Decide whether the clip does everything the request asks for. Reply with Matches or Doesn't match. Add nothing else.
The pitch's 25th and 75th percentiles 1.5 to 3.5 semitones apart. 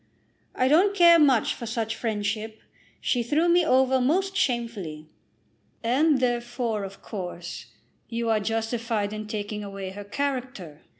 Doesn't match